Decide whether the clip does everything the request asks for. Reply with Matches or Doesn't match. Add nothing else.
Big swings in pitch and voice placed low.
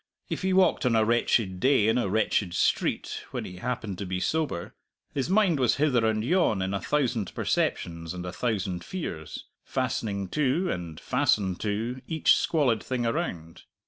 Matches